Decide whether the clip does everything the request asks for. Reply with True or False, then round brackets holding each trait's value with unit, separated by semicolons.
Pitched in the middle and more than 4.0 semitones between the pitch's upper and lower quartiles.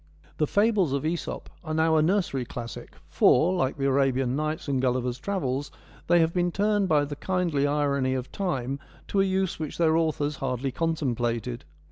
True (150 Hz; 4.6 semitones)